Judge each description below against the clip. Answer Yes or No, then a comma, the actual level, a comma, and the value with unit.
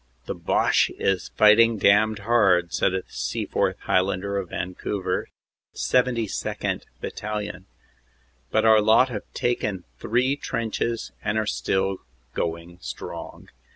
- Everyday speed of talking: No, slow, 120 wpm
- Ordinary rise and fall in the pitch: Yes, average, 3.0 semitones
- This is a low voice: Yes, low, 105 Hz